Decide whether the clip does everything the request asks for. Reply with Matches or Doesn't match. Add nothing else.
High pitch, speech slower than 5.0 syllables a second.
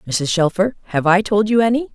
Doesn't match